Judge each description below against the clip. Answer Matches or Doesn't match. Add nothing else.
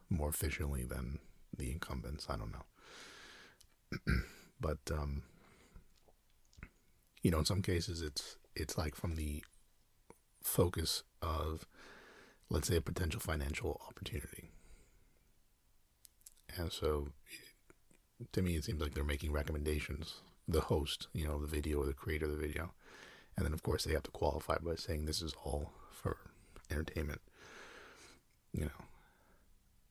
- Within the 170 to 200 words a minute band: Doesn't match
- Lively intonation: Doesn't match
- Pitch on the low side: Matches